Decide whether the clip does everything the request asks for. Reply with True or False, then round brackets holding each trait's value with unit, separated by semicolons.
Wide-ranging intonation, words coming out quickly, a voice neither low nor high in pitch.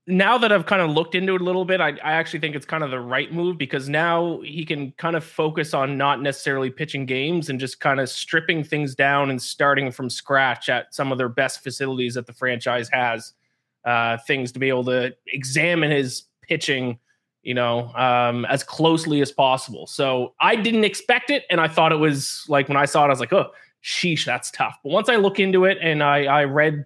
False (3.8 semitones; 230 wpm; 145 Hz)